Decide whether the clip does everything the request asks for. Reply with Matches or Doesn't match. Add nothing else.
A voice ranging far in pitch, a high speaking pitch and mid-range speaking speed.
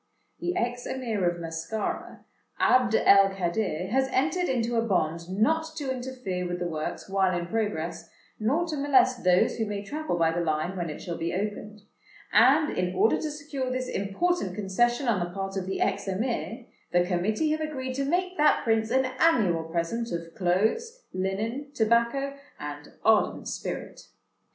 Matches